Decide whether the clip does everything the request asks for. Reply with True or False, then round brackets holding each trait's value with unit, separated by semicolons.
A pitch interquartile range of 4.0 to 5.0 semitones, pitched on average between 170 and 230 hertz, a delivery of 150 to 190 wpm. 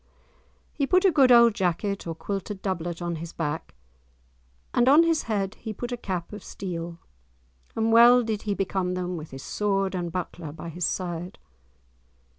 True (4.7 semitones; 190 Hz; 175 wpm)